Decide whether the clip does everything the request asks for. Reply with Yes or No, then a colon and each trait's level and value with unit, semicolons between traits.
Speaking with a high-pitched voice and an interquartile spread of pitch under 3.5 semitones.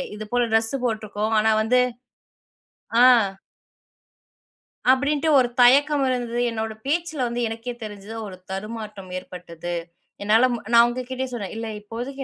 Yes: high, 230 Hz; average, 3.0 semitones